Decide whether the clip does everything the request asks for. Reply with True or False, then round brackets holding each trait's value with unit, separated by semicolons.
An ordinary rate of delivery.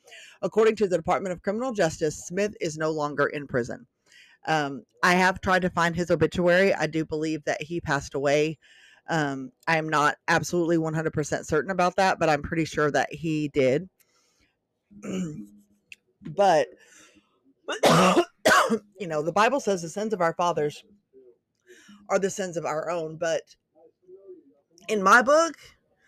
True (150 wpm)